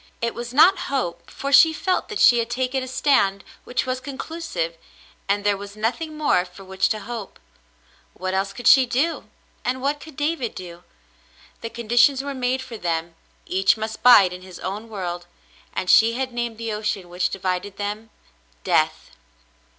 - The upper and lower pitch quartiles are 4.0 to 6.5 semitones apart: Yes, wide, 5.4 semitones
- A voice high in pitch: Yes, high, 225 Hz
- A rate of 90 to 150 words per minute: No, average, 180 wpm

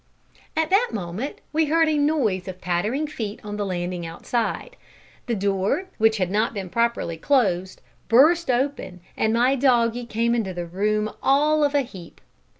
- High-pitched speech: Yes, high, 230 Hz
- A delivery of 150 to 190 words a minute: Yes, average, 165 wpm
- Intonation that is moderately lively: No, wide, 6.9 semitones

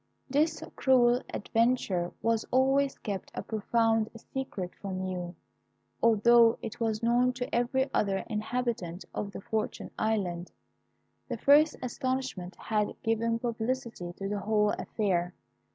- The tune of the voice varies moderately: Yes, average, 3.8 semitones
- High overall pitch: Yes, high, 225 Hz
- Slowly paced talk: Yes, slow, 125 wpm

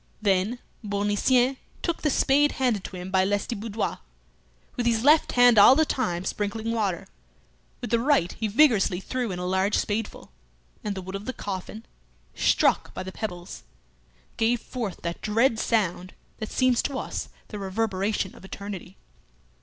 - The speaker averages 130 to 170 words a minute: Yes, average, 160 wpm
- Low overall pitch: No, high, 210 Hz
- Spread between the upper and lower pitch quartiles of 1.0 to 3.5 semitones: No, average, 4.2 semitones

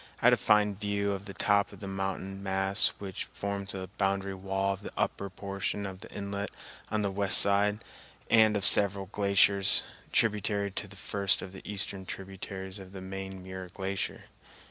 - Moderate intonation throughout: No, narrow, 0.9 semitones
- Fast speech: No, average, 185 wpm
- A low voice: Yes, low, 100 Hz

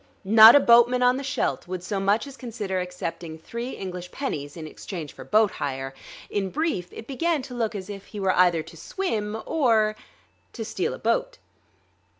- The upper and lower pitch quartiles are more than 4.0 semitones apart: Yes, wide, 5.6 semitones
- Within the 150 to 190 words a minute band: Yes, average, 185 wpm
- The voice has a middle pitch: No, high, 210 Hz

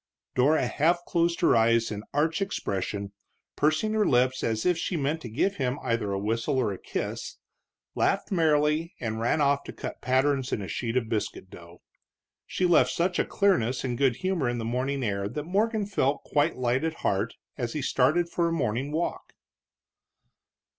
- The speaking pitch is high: No, low, 135 Hz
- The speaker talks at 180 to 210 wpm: Yes, average, 185 wpm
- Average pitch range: No, wide, 6.1 semitones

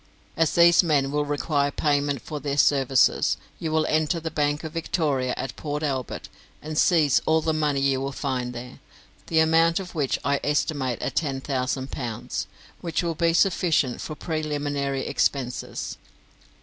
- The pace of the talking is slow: No, average, 160 wpm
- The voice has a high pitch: No, medium, 145 Hz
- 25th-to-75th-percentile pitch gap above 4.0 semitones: No, average, 2.7 semitones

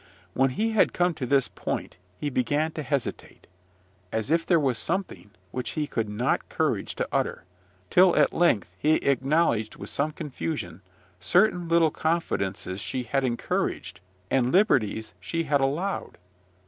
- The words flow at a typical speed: Yes, average, 150 wpm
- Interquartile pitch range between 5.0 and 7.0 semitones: Yes, wide, 5.4 semitones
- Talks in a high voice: No, medium, 140 Hz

